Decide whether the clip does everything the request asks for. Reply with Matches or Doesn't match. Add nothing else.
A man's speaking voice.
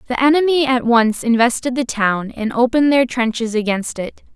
Doesn't match